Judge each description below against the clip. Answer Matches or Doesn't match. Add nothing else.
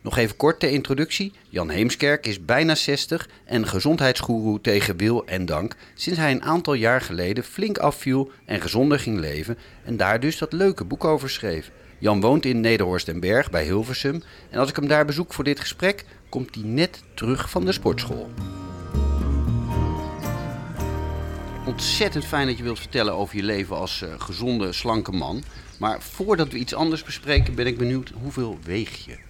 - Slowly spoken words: Doesn't match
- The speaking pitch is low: Matches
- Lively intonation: Matches